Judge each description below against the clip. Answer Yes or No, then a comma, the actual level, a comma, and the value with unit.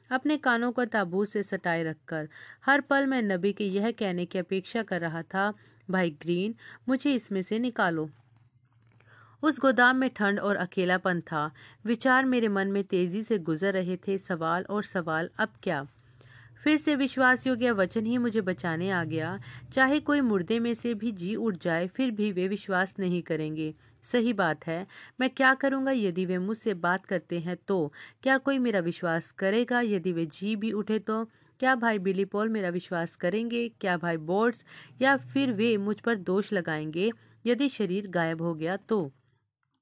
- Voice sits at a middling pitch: No, high, 195 Hz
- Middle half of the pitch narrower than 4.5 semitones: No, average, 5.3 semitones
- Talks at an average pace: Yes, average, 175 wpm